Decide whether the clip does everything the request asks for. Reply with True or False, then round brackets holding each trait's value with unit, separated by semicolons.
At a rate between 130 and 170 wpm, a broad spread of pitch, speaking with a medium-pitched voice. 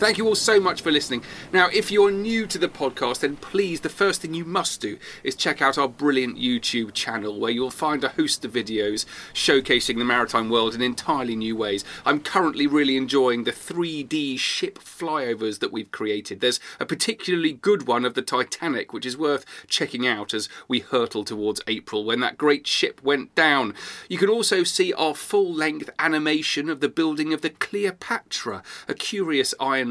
False (195 wpm; 8.3 semitones; 145 Hz)